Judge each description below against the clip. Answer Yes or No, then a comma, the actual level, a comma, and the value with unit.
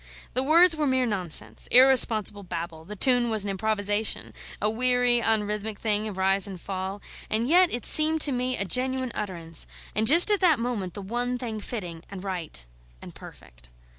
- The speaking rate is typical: Yes, average, 180 wpm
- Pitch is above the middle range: Yes, high, 215 Hz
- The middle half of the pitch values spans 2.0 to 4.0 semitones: No, average, 4.7 semitones